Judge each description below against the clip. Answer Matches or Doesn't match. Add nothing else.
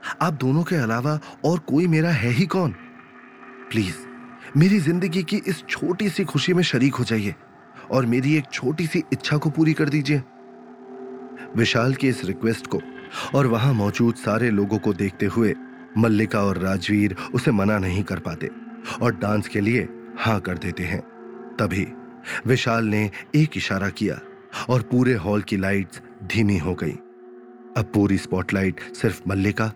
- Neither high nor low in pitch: Doesn't match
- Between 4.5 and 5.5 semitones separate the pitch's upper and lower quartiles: Matches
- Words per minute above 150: Matches